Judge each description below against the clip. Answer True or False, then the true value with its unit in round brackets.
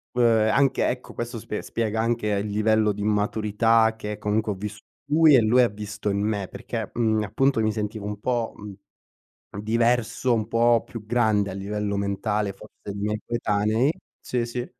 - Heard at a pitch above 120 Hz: False (110 Hz)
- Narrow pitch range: True (2.1 semitones)